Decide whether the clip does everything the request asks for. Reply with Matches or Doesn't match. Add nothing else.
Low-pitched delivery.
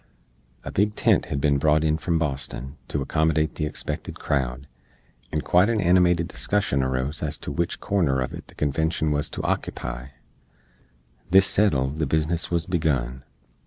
Matches